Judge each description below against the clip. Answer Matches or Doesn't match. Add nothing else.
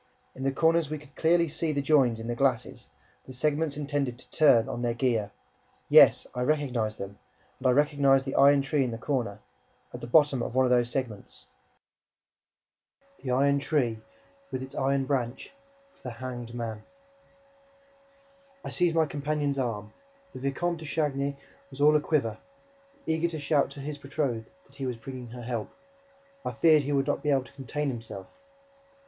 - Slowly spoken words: Doesn't match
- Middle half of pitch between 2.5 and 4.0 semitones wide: Matches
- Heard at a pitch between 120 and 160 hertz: Matches